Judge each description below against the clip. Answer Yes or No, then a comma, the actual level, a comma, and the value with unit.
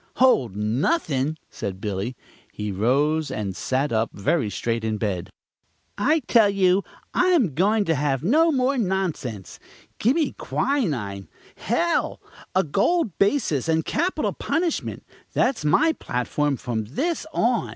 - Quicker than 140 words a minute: No, slow, 135 wpm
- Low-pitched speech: No, medium, 155 Hz